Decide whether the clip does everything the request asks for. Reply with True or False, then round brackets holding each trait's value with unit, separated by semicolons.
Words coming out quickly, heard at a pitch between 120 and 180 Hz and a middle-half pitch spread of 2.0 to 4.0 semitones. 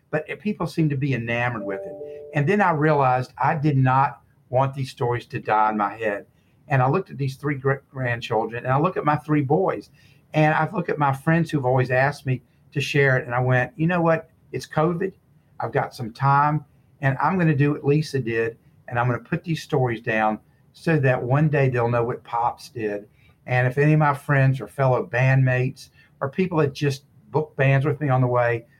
True (225 wpm; 140 Hz; 3.1 semitones)